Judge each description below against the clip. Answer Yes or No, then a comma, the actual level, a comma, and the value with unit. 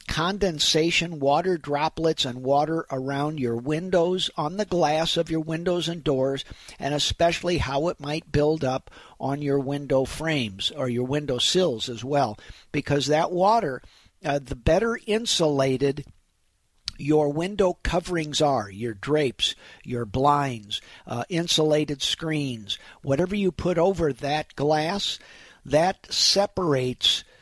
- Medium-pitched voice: Yes, medium, 150 Hz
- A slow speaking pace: Yes, slow, 130 wpm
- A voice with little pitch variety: No, average, 3.8 semitones